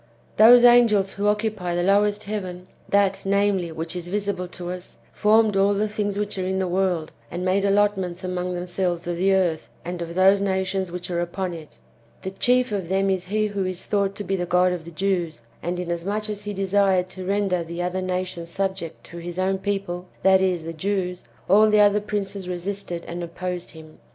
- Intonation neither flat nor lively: No, narrow, 2.3 semitones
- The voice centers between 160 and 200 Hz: Yes, high, 190 Hz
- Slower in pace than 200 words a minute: No, fast, 205 wpm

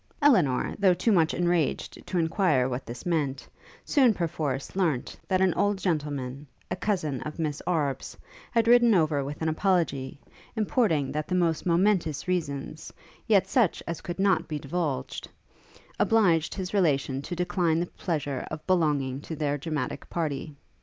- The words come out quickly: No, average, 155 wpm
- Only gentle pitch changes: No, average, 4.3 semitones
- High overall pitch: No, medium, 160 Hz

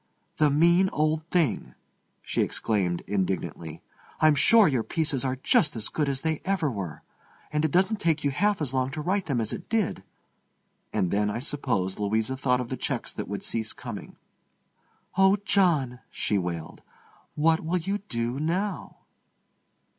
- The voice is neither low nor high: Yes, medium, 145 Hz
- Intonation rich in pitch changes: Yes, wide, 7.0 semitones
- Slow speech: No, average, 165 wpm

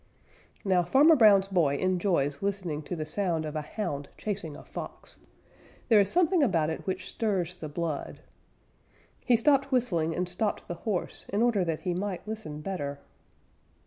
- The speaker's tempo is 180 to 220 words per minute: No, average, 165 wpm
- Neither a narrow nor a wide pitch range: Yes, average, 4.8 semitones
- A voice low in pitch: No, medium, 185 Hz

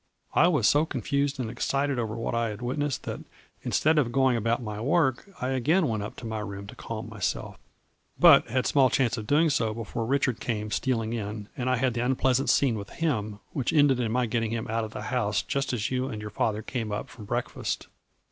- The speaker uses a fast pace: Yes, fast, 225 wpm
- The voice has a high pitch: No, low, 120 Hz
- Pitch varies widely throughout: No, average, 3.5 semitones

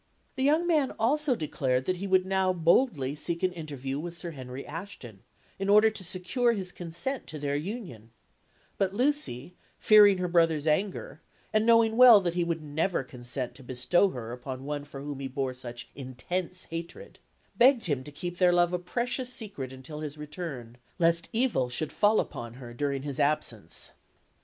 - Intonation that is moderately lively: No, wide, 6.8 semitones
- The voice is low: No, medium, 170 Hz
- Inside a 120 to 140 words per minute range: No, average, 180 wpm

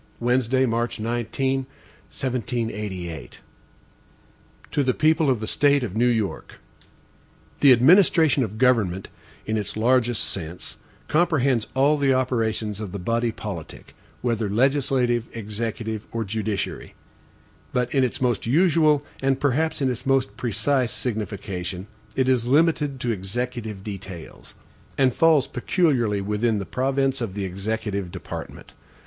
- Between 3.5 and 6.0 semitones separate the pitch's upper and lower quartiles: Yes, average, 4.0 semitones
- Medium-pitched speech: No, low, 120 Hz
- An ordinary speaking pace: No, slow, 130 wpm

